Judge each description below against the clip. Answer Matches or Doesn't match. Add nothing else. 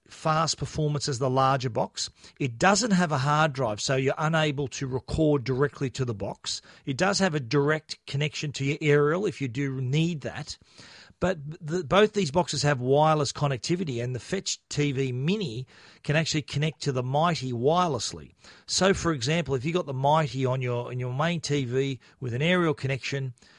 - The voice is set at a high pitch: Doesn't match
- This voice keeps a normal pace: Matches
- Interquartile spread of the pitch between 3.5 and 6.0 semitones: Doesn't match